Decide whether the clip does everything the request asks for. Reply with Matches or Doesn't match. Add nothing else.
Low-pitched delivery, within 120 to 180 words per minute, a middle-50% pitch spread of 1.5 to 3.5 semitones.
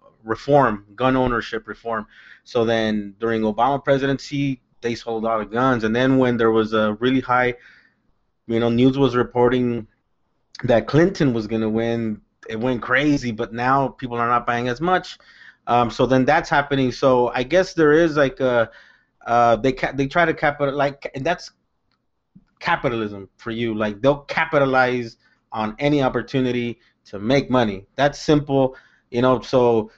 Matches